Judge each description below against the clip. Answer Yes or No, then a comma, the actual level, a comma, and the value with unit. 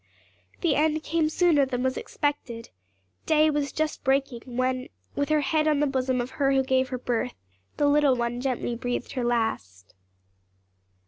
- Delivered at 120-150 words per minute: No, average, 170 wpm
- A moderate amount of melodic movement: Yes, average, 3.1 semitones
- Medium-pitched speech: No, very high, 265 Hz